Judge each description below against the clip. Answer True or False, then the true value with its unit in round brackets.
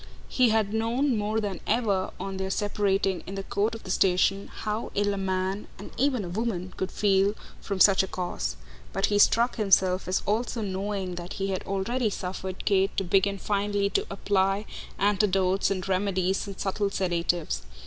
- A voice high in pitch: True (195 Hz)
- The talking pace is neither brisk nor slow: True (180 wpm)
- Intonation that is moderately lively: False (1.7 semitones)